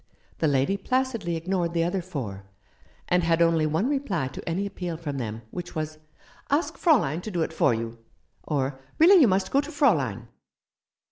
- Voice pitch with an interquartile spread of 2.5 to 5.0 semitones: No, wide, 5.6 semitones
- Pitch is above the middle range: No, medium, 170 Hz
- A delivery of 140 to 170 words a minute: No, average, 180 wpm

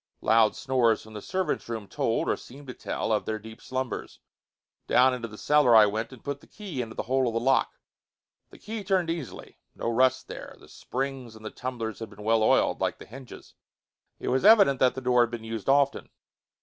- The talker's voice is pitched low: Yes, low, 125 Hz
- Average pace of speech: No, fast, 215 wpm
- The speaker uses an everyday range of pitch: Yes, average, 3.3 semitones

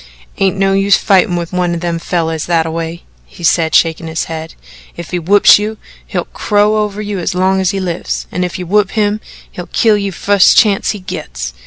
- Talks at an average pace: No, fast, 210 wpm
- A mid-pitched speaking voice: Yes, medium, 180 Hz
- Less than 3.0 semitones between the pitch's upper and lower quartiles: No, average, 3.3 semitones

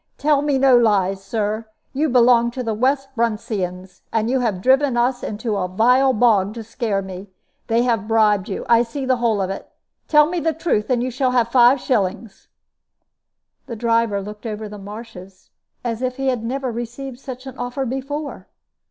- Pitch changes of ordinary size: Yes, average, 3.6 semitones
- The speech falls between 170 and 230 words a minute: Yes, average, 185 wpm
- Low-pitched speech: No, high, 235 Hz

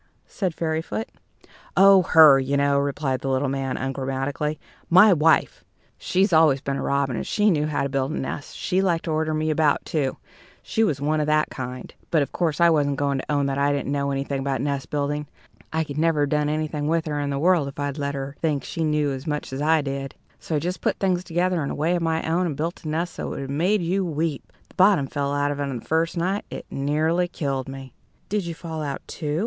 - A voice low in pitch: No, medium, 150 Hz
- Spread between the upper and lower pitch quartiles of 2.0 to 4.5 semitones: Yes, average, 2.9 semitones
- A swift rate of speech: Yes, fast, 240 wpm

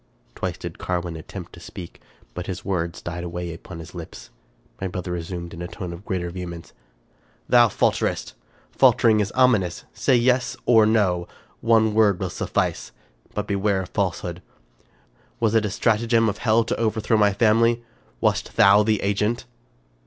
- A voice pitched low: Yes, low, 100 Hz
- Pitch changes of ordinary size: Yes, average, 4.1 semitones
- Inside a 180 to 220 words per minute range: No, average, 165 wpm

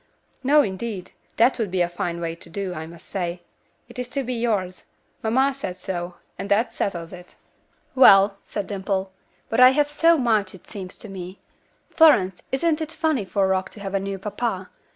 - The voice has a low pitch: No, high, 195 Hz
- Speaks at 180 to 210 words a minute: Yes, average, 195 wpm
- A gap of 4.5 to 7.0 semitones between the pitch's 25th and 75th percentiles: Yes, average, 4.8 semitones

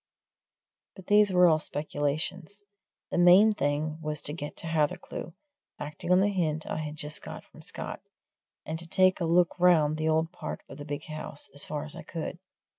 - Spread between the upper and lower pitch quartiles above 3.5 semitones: No, average, 2.9 semitones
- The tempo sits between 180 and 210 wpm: Yes, average, 190 wpm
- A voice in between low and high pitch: Yes, medium, 160 Hz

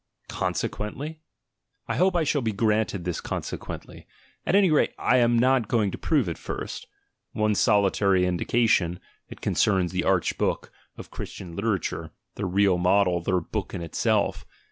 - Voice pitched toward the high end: No, low, 100 Hz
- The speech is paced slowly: No, average, 155 wpm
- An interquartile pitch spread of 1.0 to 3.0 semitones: No, average, 4.7 semitones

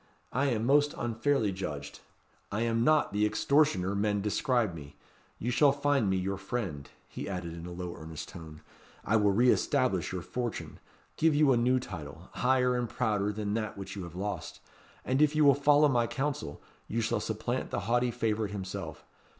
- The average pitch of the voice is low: Yes, low, 110 Hz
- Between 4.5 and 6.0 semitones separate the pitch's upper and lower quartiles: Yes, average, 5.2 semitones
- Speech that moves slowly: No, average, 185 wpm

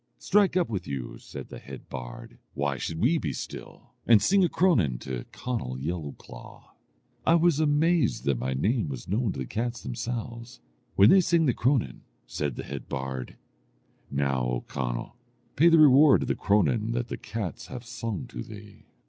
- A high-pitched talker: No, low, 110 Hz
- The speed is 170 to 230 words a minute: Yes, average, 180 wpm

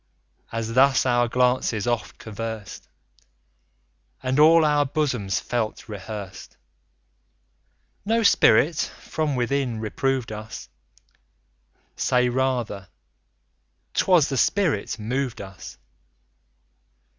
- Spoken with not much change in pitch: No, average, 4.0 semitones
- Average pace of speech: No, slow, 85 wpm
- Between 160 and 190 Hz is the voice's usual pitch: No, low, 125 Hz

